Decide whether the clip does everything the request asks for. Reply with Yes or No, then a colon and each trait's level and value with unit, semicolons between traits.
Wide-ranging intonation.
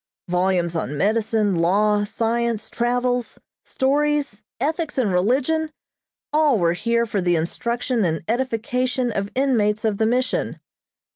No: average, 4.1 semitones